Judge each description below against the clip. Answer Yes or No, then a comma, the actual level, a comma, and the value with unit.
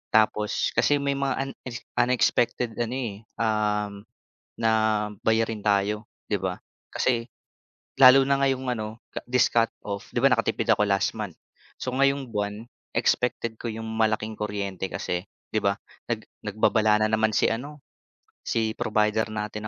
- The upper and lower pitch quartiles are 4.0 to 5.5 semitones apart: No, average, 2.7 semitones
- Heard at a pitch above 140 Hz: No, low, 110 Hz